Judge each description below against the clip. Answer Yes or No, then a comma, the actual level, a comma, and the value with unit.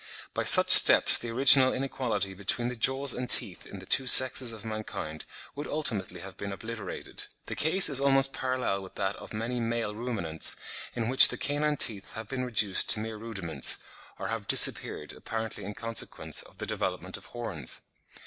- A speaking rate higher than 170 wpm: Yes, average, 180 wpm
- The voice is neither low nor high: No, low, 115 Hz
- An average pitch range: Yes, average, 4.3 semitones